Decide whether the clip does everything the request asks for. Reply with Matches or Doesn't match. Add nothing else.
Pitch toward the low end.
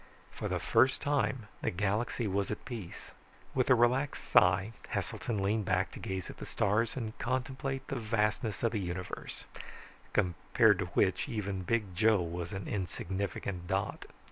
Matches